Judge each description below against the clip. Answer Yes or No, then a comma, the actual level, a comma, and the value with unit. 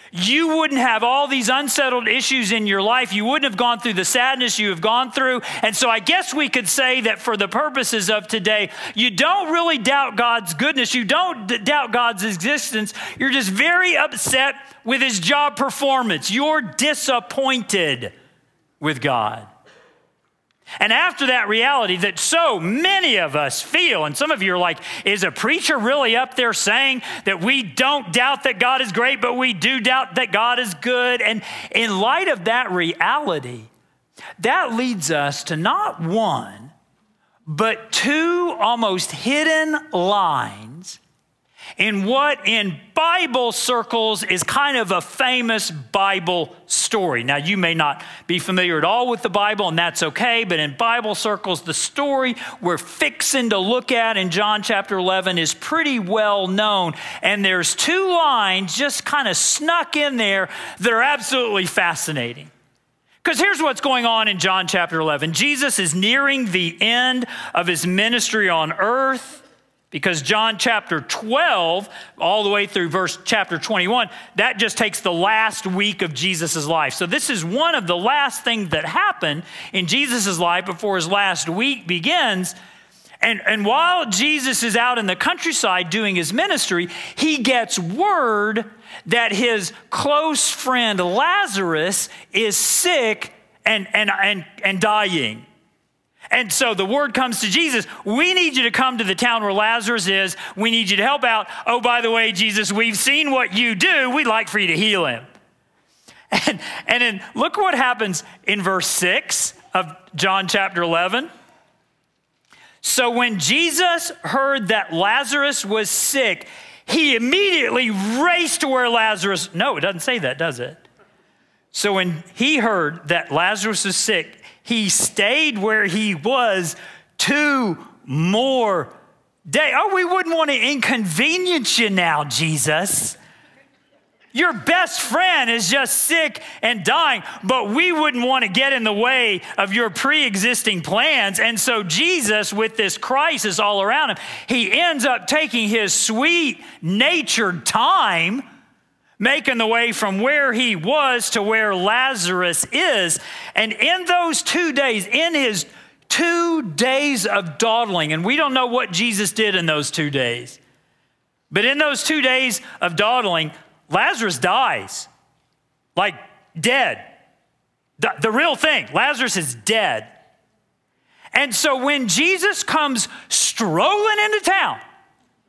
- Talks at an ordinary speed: Yes, average, 155 wpm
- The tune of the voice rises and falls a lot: Yes, wide, 5.8 semitones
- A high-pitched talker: Yes, high, 230 Hz